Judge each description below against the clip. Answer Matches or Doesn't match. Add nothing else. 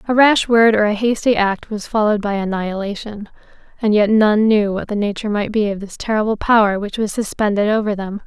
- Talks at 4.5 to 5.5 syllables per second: Doesn't match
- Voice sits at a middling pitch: Doesn't match